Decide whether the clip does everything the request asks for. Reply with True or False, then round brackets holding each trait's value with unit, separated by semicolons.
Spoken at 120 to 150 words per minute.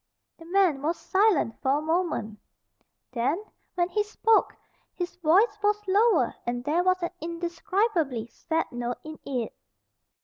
True (140 wpm)